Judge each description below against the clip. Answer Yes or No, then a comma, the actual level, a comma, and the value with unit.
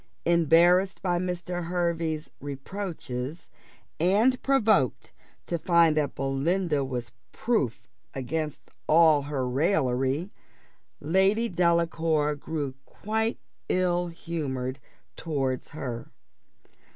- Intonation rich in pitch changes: No, average, 4.4 semitones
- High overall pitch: No, medium, 165 Hz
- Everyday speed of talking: No, slow, 90 wpm